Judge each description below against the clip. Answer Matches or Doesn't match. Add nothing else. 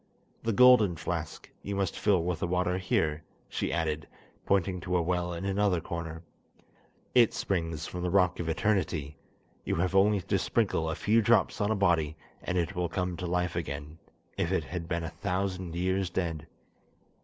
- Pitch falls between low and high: Doesn't match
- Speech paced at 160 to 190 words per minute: Matches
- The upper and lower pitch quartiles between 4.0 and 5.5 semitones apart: Doesn't match